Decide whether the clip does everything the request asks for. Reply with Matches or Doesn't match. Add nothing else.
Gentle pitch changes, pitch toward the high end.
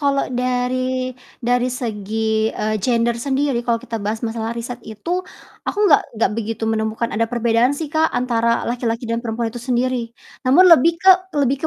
Matches